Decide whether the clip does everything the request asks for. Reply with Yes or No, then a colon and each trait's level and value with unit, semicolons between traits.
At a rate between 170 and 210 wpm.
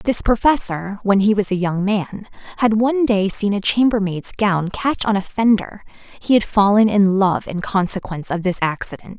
Yes: average, 190 wpm